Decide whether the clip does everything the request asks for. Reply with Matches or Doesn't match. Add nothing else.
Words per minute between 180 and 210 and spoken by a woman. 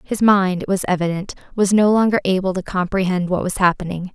Matches